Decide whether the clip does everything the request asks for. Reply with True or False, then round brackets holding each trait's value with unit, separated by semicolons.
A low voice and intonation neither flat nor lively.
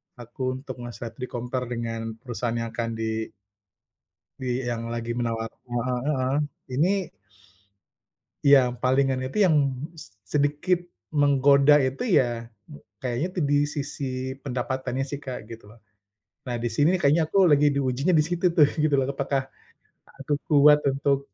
True (130 Hz; 3.2 semitones)